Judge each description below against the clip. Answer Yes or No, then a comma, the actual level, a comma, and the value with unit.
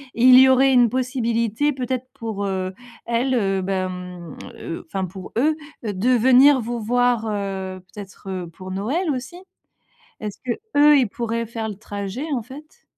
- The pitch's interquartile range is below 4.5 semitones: No, average, 4.8 semitones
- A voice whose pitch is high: Yes, high, 230 Hz